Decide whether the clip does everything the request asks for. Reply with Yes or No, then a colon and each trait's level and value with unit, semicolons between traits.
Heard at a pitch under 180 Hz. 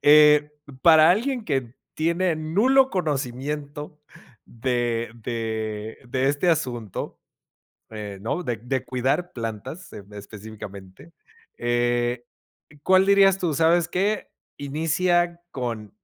Yes: medium, 140 Hz